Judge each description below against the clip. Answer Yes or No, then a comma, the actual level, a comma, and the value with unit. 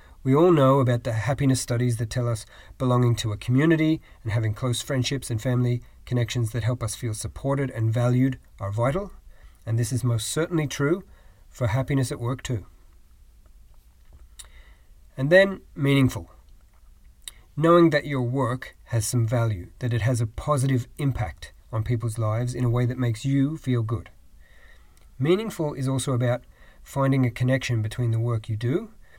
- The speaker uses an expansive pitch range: No, average, 3.1 semitones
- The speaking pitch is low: Yes, low, 125 Hz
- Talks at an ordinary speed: Yes, average, 165 wpm